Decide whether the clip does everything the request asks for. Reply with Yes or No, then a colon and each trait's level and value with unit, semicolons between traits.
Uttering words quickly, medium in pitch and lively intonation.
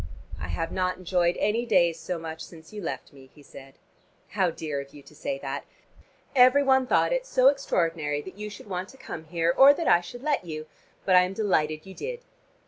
Yes: fast, 220 wpm; medium, 180 Hz; wide, 7.3 semitones